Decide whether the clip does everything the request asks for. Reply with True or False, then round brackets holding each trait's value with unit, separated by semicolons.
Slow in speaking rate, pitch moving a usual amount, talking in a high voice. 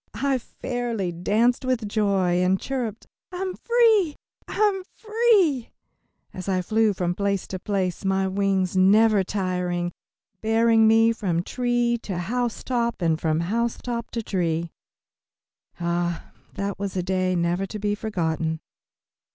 True (130 wpm; 4.6 semitones; 200 Hz)